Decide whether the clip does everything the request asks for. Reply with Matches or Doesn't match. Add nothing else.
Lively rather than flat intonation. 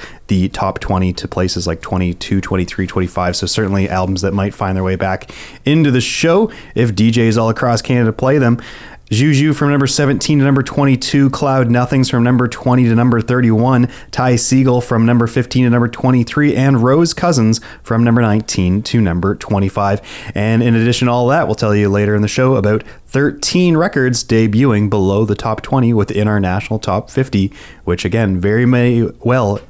Doesn't match